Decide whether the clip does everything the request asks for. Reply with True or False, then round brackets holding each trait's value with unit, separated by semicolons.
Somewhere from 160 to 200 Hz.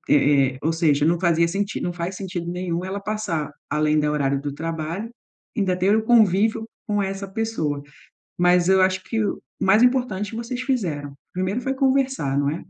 True (185 Hz)